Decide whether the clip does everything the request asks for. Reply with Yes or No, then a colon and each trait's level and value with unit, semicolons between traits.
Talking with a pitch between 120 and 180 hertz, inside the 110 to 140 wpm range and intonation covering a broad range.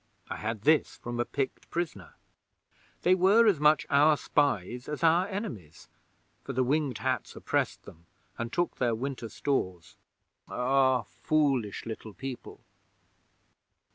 No: low, 135 Hz; slow, 135 wpm; average, 5.0 semitones